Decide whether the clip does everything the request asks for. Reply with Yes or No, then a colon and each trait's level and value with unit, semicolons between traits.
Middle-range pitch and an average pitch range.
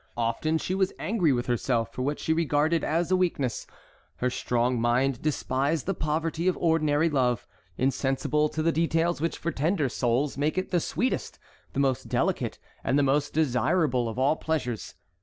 Yes: medium, 150 Hz; average, 4.3 semitones